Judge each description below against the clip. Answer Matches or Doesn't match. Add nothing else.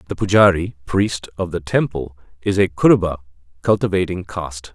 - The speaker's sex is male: Matches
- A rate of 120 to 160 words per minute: Matches